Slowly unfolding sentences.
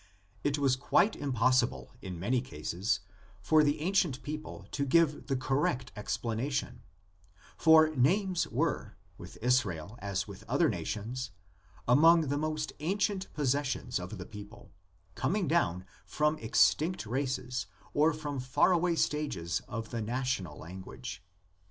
Yes: slow, 130 wpm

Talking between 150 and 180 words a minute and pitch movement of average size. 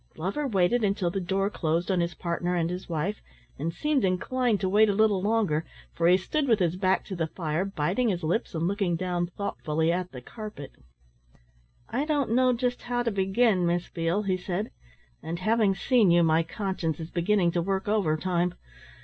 No: average, 190 wpm; average, 3.8 semitones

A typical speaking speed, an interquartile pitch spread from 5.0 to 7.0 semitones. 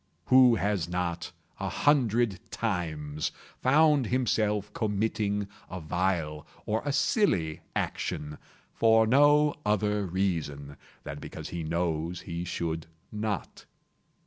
No: slow, 110 wpm; average, 5.3 semitones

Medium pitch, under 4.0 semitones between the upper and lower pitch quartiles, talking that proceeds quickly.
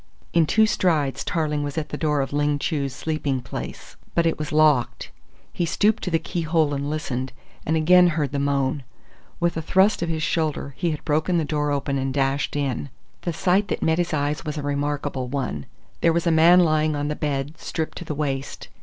Yes: medium, 150 Hz; narrow, 2.5 semitones; fast, 215 wpm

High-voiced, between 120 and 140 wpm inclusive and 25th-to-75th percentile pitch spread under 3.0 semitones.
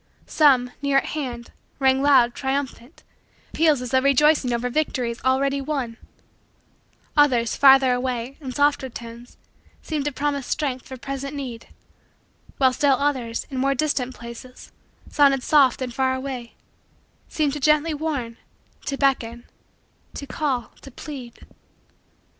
Yes: very high, 265 Hz; slow, 135 wpm; narrow, 2.5 semitones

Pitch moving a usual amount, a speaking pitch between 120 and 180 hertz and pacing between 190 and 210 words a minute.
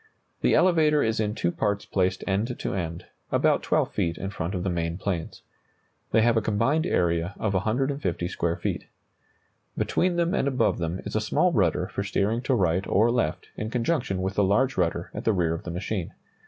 No: average, 5.0 semitones; low, 100 Hz; average, 200 wpm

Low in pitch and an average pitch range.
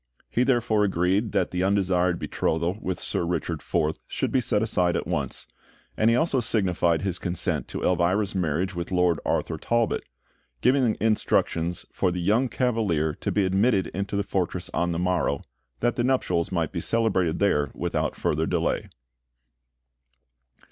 Yes: very low, 95 Hz; average, 4.0 semitones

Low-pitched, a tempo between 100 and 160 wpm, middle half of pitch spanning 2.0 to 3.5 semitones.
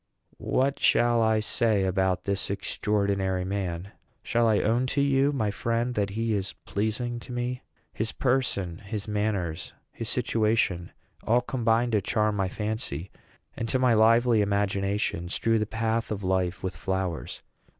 Yes: low, 105 Hz; average, 150 wpm; average, 3.1 semitones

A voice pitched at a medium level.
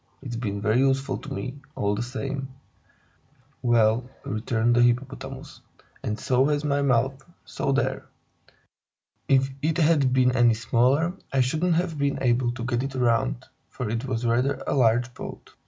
No: low, 125 Hz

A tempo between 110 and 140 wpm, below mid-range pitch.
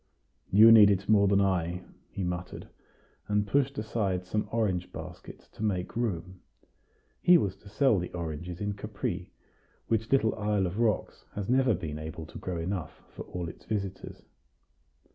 No: average, 160 wpm; low, 100 Hz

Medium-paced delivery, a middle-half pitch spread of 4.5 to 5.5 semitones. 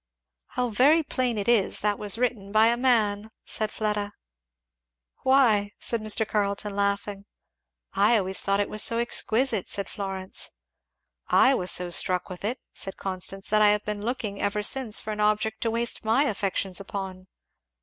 No: average, 170 wpm; narrow, 2.5 semitones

